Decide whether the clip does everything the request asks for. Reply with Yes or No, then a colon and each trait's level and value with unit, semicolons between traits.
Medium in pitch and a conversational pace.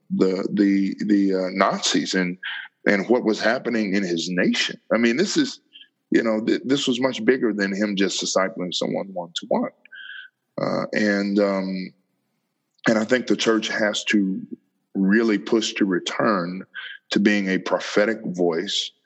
No: low, 105 Hz; average, 160 wpm